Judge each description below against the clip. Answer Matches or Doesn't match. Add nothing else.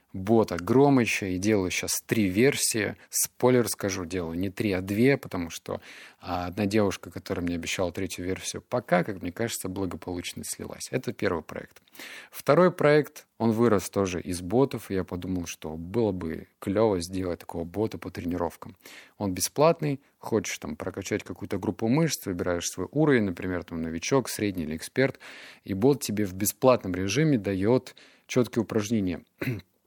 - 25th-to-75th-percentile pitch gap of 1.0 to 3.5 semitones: Doesn't match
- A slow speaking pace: Doesn't match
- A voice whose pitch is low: Matches